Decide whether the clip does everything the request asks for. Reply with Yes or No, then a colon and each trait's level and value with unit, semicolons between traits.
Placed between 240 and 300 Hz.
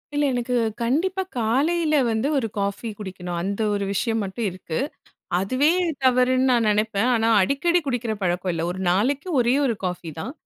No: high, 230 Hz